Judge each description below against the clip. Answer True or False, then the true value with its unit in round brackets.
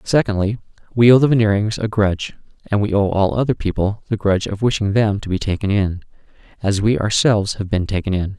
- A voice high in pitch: False (105 Hz)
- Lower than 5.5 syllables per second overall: False (6.0 syllables/s)